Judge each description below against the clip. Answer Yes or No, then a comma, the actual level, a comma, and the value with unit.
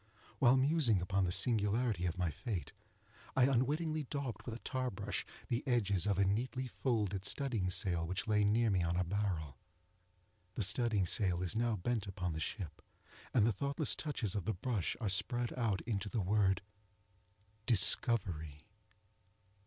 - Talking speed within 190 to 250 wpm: No, average, 160 wpm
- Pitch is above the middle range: No, low, 105 Hz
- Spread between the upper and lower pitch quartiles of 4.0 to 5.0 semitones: Yes, average, 4.7 semitones